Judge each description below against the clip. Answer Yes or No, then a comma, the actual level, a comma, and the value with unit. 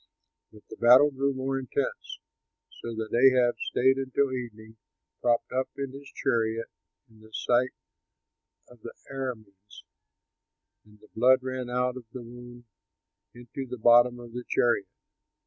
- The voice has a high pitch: No, low, 120 Hz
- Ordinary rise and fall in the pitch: No, narrow, 2.2 semitones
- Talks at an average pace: Yes, average, 145 wpm